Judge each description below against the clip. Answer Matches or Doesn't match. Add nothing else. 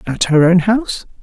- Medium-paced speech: Matches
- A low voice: Doesn't match